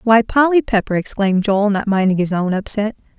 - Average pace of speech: Yes, average, 190 wpm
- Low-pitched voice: No, high, 210 Hz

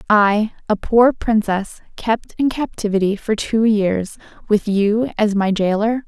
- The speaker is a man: No, female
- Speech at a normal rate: Yes, average, 150 wpm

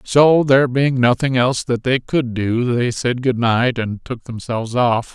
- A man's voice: Yes, male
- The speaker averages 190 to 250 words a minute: Yes, average, 200 wpm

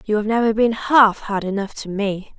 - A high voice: Yes, high, 215 Hz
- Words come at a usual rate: No, fast, 225 wpm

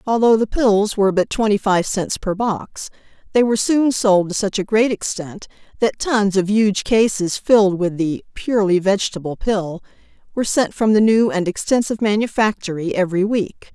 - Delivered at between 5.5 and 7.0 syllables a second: No, 5.1 syllables/s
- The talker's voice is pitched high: Yes, high, 205 Hz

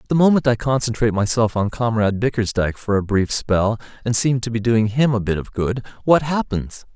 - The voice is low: Yes, low, 115 Hz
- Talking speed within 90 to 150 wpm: No, fast, 205 wpm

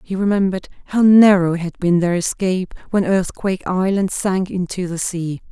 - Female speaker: Yes, female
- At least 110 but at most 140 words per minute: No, average, 165 wpm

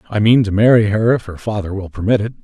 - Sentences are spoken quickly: Yes, fast, 270 wpm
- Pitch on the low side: Yes, low, 105 Hz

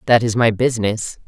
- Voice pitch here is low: Yes, low, 115 Hz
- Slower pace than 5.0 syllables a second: No, 5.6 syllables/s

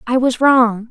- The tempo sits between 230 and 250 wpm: No, average, 200 wpm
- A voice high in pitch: Yes, high, 245 Hz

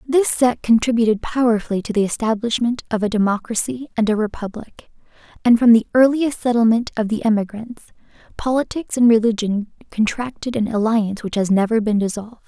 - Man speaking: No, female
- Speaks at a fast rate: No, average, 155 wpm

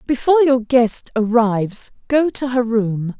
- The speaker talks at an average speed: Yes, average, 150 wpm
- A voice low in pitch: No, high, 240 Hz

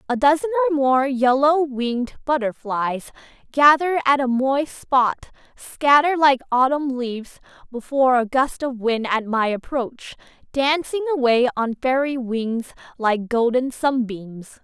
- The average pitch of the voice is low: No, very high, 260 Hz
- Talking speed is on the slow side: Yes, slow, 130 wpm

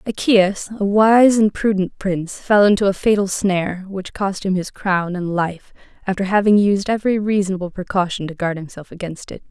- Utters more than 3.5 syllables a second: Yes, 5.2 syllables/s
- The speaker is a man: No, female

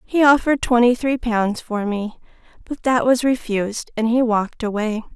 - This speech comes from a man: No, female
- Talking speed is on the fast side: No, average, 175 wpm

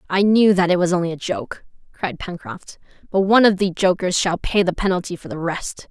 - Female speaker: Yes, female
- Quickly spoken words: Yes, fast, 225 wpm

